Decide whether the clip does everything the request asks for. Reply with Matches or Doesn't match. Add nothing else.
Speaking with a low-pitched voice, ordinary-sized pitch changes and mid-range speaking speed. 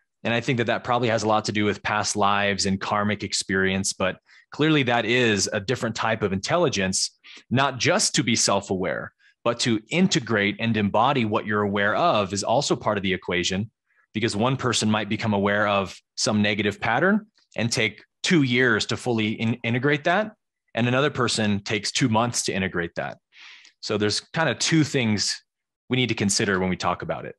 Matches